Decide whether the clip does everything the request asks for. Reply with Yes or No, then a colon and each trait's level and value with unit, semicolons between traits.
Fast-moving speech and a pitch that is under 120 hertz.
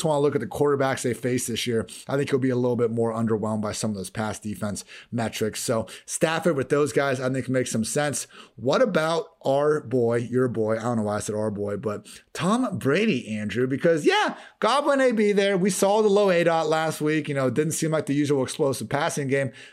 No: fast, 235 wpm; low, 135 Hz